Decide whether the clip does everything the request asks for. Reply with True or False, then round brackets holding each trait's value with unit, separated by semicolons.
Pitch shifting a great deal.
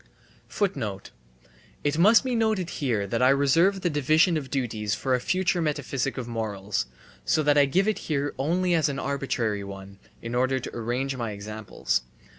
True (6.0 semitones)